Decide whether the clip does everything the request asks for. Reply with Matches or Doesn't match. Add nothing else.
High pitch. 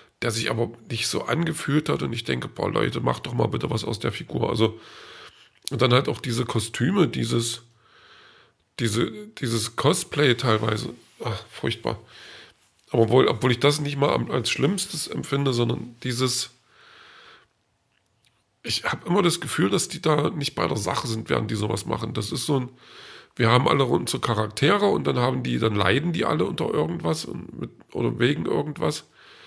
Doesn't match